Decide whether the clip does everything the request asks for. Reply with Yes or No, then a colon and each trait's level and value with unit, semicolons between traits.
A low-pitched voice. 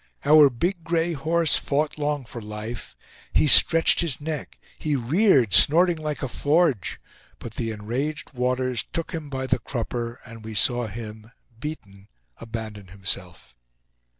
Yes: low, 130 Hz